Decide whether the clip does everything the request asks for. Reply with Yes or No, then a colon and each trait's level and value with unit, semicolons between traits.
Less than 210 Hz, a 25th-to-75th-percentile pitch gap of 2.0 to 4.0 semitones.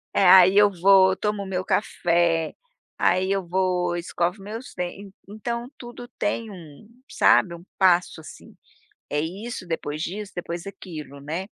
Yes: medium, 185 Hz; average, 2.8 semitones